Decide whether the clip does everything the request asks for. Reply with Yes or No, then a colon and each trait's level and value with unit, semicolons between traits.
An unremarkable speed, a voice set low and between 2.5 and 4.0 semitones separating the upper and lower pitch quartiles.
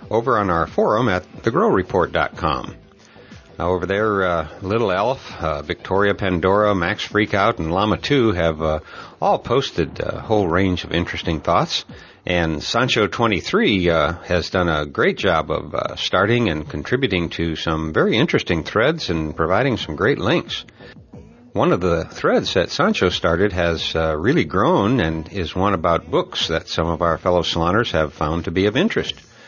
Yes: average, 165 wpm; very low, 85 Hz; average, 3.4 semitones